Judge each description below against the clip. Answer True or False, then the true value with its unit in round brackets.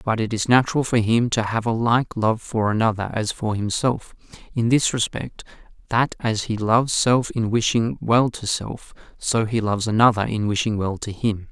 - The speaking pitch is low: True (115 Hz)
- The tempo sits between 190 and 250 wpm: True (200 wpm)